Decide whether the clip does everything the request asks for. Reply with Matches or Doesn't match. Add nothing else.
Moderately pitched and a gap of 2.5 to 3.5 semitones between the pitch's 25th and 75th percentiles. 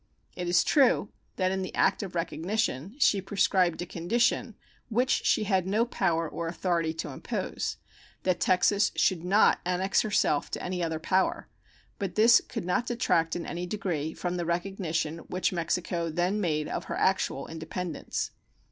Matches